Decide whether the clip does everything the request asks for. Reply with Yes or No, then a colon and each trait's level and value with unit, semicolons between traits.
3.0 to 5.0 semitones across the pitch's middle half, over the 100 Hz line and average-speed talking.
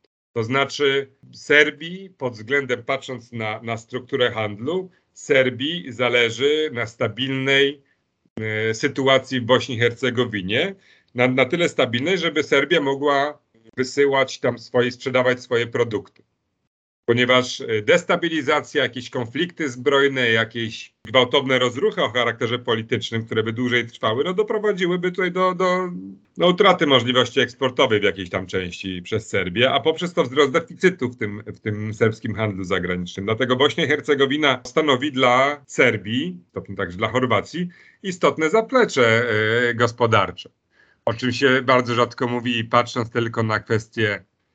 Yes: average, 4.1 semitones; low, 125 Hz; average, 135 wpm